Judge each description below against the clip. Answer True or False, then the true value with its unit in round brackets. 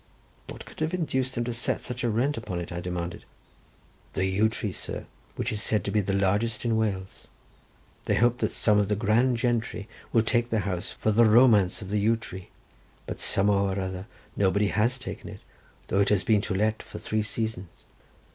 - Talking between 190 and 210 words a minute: True (205 wpm)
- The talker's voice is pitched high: False (105 Hz)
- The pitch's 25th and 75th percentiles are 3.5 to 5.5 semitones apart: False (3.1 semitones)